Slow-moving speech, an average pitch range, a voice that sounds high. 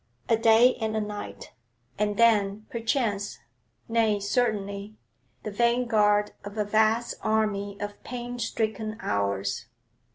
No: slow, 120 wpm; narrow, 2.1 semitones; high, 215 Hz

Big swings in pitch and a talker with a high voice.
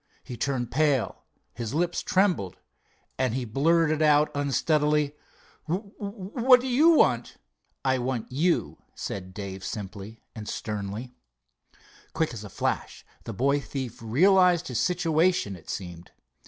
No: wide, 7.5 semitones; medium, 140 Hz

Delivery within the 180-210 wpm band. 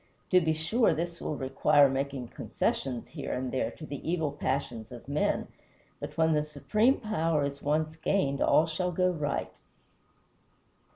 No: average, 160 wpm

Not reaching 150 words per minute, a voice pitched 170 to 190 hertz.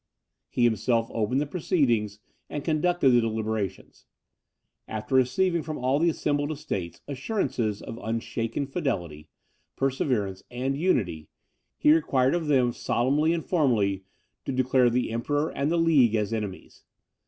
No: slow, 135 wpm; low, 130 Hz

